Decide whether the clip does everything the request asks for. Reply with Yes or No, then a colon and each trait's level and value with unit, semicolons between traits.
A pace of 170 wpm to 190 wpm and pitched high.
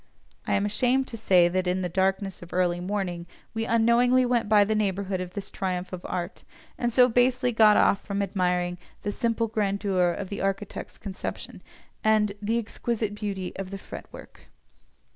Yes: average, 180 wpm; high, 200 Hz